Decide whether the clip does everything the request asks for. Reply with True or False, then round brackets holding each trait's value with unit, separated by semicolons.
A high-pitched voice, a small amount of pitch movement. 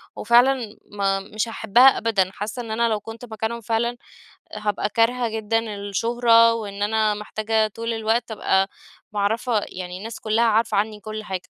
True (220 Hz; 1.8 semitones)